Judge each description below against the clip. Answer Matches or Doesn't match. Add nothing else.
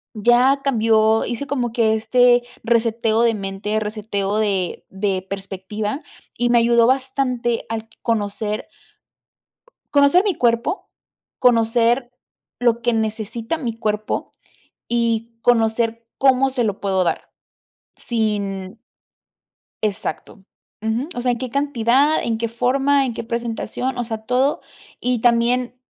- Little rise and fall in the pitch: Matches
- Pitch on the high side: Matches